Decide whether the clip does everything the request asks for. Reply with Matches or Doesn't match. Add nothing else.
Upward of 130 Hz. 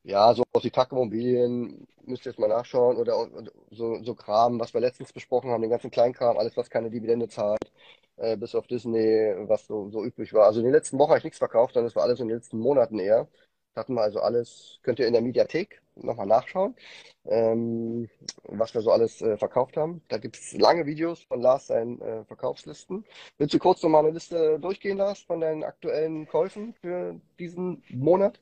Matches